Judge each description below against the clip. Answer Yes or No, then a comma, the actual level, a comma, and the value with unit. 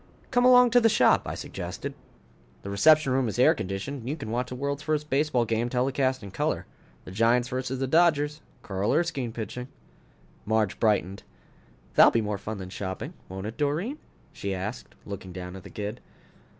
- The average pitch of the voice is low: Yes, low, 125 Hz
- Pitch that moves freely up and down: Yes, wide, 6.0 semitones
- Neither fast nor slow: Yes, average, 185 wpm